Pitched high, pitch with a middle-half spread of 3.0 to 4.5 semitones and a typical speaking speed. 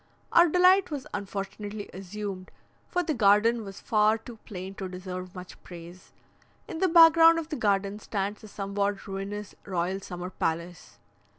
Yes: high, 200 Hz; average, 3.5 semitones; average, 160 wpm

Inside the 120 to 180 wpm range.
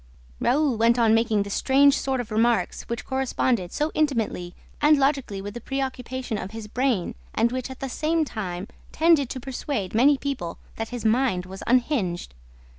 Yes: average, 175 wpm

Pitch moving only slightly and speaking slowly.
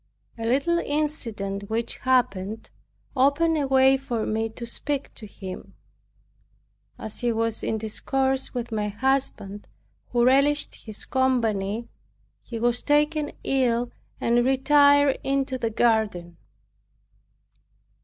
No: average, 3.6 semitones; slow, 115 wpm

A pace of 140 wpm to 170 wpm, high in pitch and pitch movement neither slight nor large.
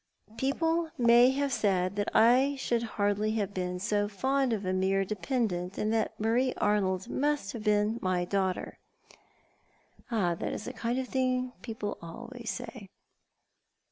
Yes: average, 155 wpm; high, 220 Hz; average, 4.3 semitones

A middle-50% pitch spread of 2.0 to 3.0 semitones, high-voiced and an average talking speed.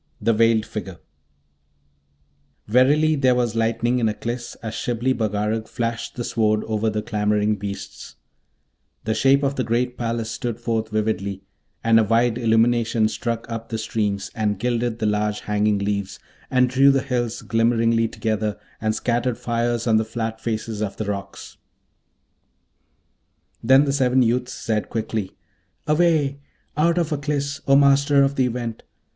No: narrow, 2.4 semitones; low, 115 Hz; average, 150 wpm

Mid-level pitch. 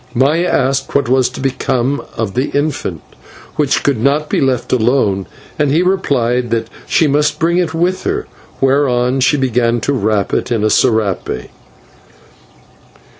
No: low, 130 Hz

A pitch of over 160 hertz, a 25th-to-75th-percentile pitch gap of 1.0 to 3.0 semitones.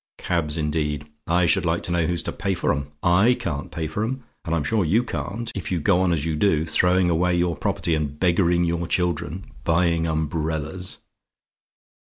No: very low, 85 Hz; narrow, 2.5 semitones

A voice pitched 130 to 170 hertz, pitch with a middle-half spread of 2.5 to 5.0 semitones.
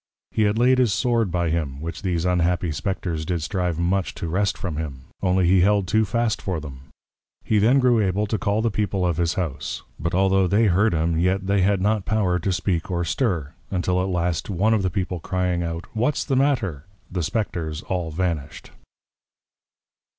No: very low, 90 Hz; average, 3.5 semitones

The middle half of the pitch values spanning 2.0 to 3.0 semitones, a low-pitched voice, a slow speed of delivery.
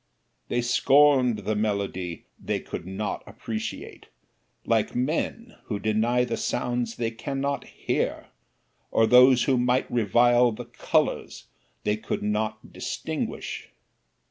Yes: narrow, 2.5 semitones; low, 120 Hz; slow, 120 wpm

